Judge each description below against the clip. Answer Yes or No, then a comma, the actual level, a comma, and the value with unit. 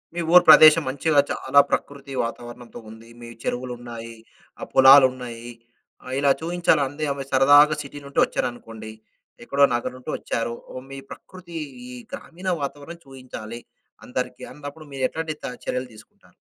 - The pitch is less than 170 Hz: Yes, low, 135 Hz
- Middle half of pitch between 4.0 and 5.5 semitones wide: No, average, 3.3 semitones